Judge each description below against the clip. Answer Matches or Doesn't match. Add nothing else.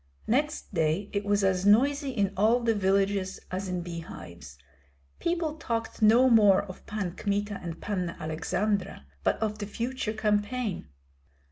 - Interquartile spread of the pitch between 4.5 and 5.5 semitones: Doesn't match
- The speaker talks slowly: Doesn't match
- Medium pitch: Doesn't match